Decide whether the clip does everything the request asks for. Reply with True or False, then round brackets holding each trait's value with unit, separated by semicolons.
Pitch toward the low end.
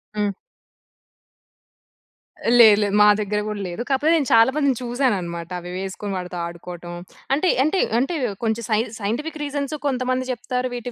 False (235 Hz)